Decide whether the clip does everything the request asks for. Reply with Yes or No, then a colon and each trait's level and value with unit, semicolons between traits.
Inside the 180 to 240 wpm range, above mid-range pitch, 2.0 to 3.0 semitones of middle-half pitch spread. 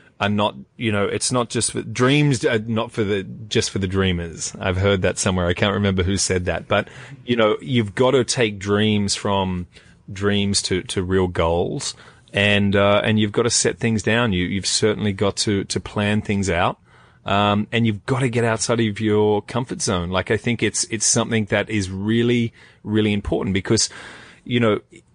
No: average, 200 wpm; low, 105 Hz; narrow, 2.6 semitones